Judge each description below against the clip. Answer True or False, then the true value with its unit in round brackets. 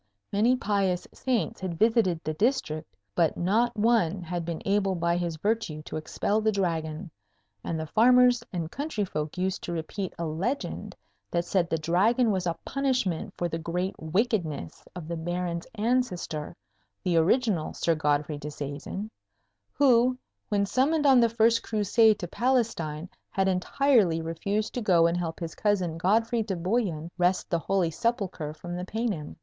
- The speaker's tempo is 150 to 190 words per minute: True (160 wpm)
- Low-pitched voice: False (185 Hz)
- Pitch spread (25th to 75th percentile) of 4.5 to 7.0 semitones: True (5.3 semitones)